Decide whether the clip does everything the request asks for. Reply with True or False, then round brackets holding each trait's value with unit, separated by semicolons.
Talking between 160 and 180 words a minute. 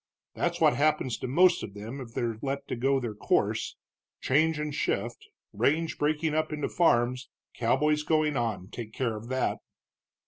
True (165 wpm)